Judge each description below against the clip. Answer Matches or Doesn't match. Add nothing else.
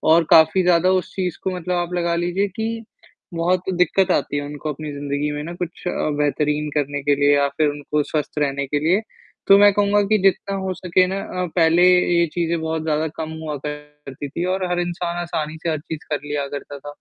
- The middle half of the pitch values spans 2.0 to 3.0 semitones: Doesn't match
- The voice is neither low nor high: Matches